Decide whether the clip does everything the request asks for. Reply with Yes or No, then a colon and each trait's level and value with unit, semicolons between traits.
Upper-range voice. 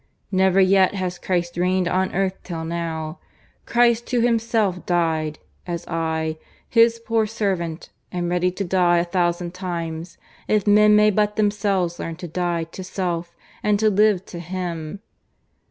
No: medium, 180 Hz